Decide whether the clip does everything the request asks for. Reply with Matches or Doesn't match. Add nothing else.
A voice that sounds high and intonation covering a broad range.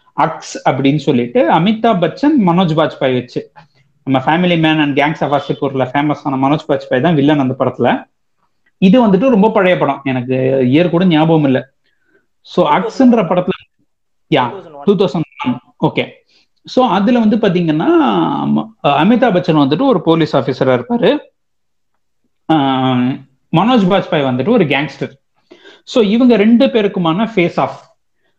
Doesn't match